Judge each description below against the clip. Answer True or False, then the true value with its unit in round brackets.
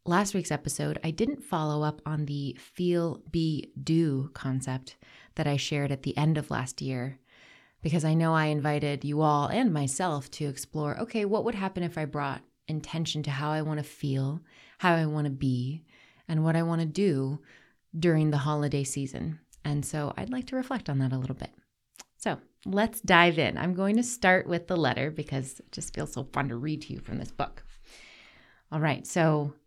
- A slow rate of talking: False (200 wpm)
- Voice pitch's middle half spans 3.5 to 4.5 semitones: False (3.0 semitones)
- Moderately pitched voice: True (150 Hz)